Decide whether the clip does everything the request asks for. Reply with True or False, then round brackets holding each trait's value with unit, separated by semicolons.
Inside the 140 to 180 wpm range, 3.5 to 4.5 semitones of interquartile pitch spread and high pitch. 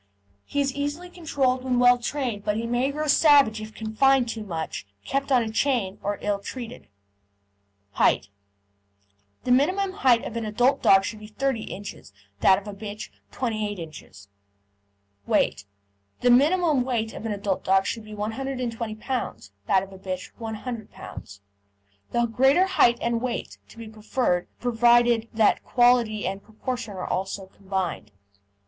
True (155 wpm; 3.8 semitones; 230 Hz)